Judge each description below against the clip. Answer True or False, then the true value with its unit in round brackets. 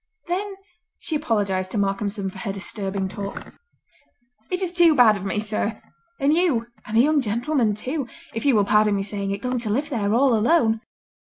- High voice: True (220 Hz)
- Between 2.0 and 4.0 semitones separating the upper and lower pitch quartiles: False (5.6 semitones)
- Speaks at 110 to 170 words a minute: False (180 wpm)